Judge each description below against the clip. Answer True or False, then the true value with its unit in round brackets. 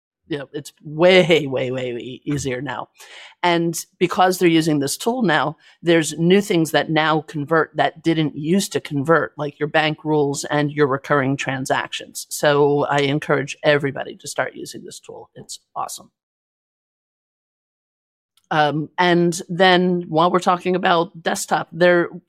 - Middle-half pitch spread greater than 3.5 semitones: False (3.2 semitones)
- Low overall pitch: False (155 Hz)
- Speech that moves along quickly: False (150 wpm)